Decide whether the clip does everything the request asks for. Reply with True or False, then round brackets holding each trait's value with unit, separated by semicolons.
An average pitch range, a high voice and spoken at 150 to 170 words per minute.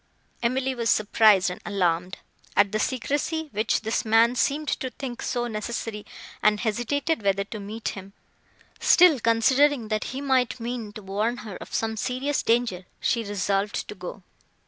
True (3.6 semitones; 225 Hz; 160 wpm)